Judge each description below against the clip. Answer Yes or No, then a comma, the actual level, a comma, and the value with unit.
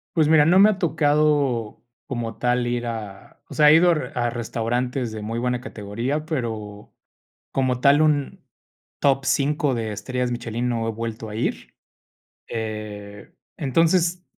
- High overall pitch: No, low, 125 Hz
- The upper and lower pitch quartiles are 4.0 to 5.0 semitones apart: Yes, average, 4.6 semitones